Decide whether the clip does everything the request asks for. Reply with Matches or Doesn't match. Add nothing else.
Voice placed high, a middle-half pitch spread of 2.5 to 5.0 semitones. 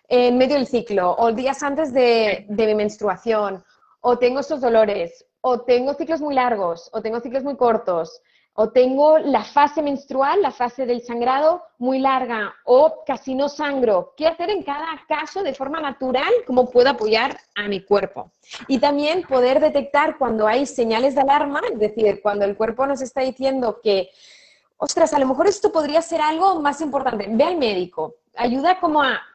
Matches